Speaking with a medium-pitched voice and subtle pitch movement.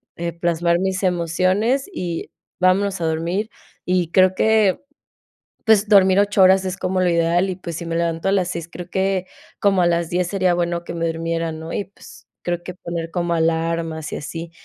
Yes: medium, 175 Hz; narrow, 2.1 semitones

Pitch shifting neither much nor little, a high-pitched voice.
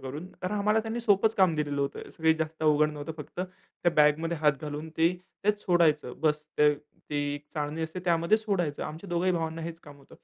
No: average, 3.2 semitones; medium, 160 Hz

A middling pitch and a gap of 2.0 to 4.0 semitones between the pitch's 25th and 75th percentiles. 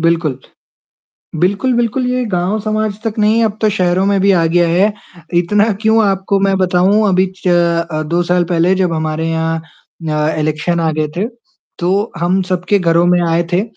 Yes: medium, 180 Hz; average, 3.4 semitones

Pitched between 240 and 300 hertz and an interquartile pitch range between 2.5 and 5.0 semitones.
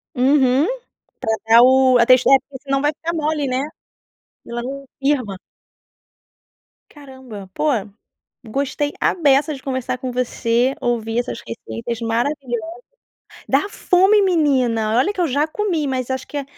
Yes: very high, 265 Hz; average, 3.3 semitones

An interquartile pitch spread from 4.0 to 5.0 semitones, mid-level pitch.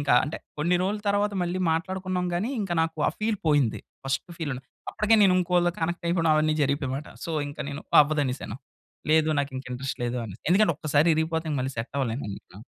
Yes: average, 4.7 semitones; medium, 155 Hz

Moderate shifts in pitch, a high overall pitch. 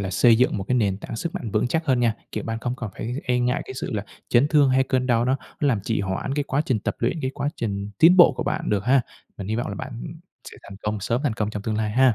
No: average, 3.8 semitones; low, 120 Hz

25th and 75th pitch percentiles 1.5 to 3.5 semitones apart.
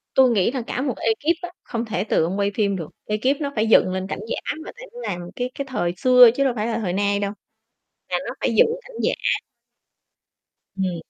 No: average, 4.8 semitones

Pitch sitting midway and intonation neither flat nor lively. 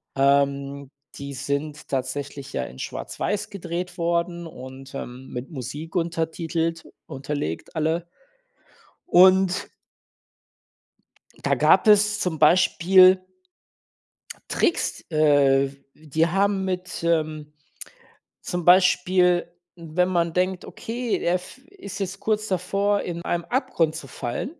Yes: medium, 170 Hz; average, 4.4 semitones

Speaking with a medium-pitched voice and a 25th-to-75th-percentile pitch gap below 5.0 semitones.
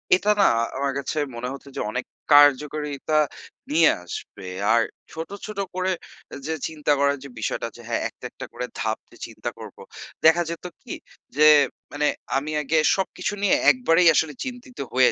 Yes: medium, 155 Hz; average, 4.4 semitones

